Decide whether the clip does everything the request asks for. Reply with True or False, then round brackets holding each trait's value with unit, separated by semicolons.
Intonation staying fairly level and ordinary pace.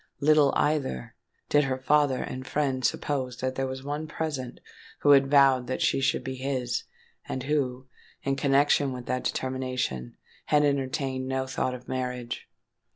True (1.7 semitones; 160 wpm)